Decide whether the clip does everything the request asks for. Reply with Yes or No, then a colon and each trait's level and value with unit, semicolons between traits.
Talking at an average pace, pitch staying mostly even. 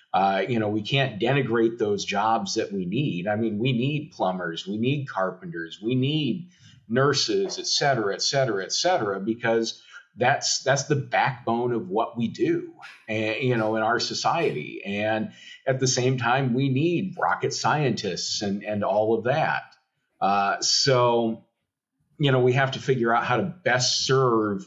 No: average, 170 wpm; average, 4.0 semitones